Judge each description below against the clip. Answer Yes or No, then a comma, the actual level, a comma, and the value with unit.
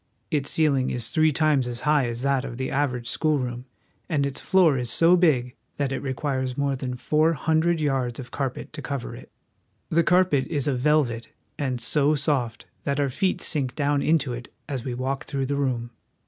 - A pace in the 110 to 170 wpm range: No, average, 200 wpm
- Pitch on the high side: No, medium, 140 Hz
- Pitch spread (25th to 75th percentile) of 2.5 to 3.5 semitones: Yes, average, 3.2 semitones